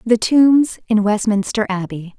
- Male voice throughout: No, female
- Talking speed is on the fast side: No, slow, 135 wpm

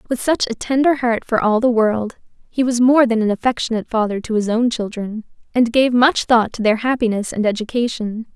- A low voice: No, high, 230 Hz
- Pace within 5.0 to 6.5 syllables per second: Yes, 5.5 syllables/s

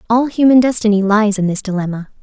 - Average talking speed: Yes, average, 190 wpm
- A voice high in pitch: Yes, high, 215 Hz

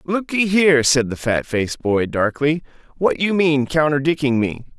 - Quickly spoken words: No, average, 165 wpm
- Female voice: No, male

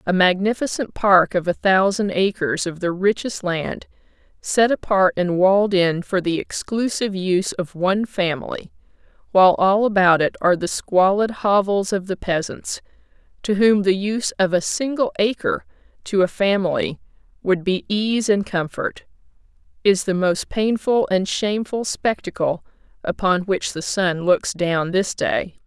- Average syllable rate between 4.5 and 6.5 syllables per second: Yes, 4.6 syllables/s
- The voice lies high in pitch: Yes, high, 195 Hz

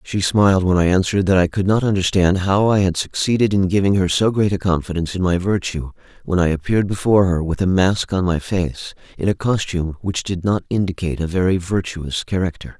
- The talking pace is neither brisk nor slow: No, fast, 215 wpm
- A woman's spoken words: No, male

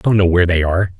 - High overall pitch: No, very low, 90 Hz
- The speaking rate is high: Yes, fast, 365 wpm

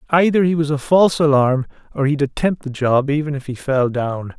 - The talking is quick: Yes, fast, 220 wpm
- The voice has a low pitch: No, medium, 145 Hz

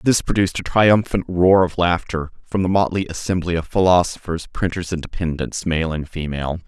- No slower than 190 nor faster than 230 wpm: No, average, 170 wpm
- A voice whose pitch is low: Yes, very low, 85 Hz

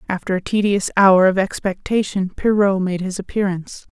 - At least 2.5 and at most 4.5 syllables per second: No, 5.3 syllables/s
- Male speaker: No, female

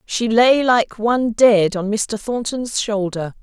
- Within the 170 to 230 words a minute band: No, average, 155 wpm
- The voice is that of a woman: Yes, female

